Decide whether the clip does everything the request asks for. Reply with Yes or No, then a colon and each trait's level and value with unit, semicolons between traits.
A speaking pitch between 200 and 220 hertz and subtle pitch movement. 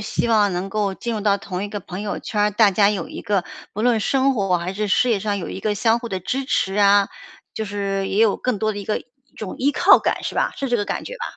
Yes: high, 205 Hz; narrow, 2.3 semitones